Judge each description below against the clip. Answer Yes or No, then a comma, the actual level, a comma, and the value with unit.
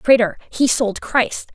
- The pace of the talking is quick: No, average, 155 wpm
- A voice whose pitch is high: Yes, high, 235 Hz